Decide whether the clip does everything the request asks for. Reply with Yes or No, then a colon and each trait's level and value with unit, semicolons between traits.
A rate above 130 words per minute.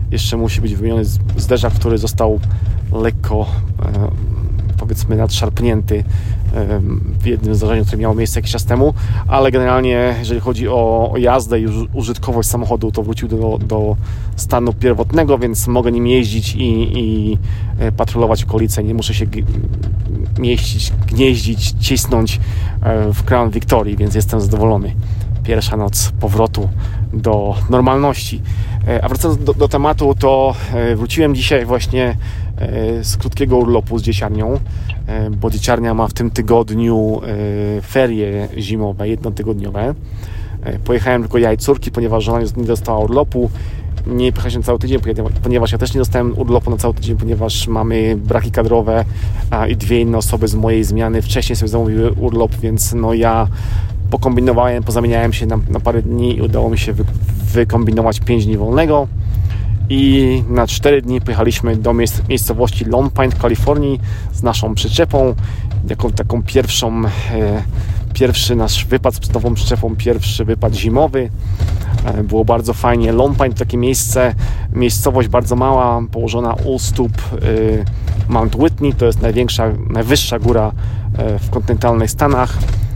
Yes: average, 145 wpm